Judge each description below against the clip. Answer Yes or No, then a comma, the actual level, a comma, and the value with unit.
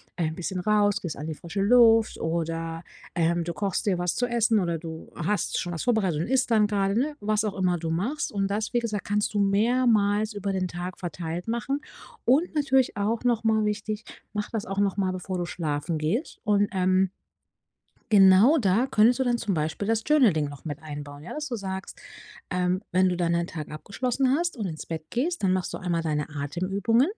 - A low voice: No, high, 195 Hz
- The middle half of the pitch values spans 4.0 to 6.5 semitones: Yes, average, 4.7 semitones